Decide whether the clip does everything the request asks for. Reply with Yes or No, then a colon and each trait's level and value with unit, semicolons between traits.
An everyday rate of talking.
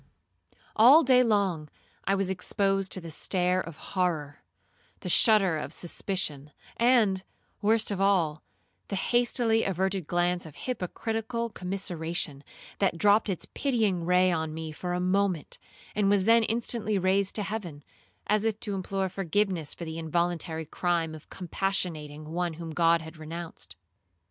Yes: average, 145 wpm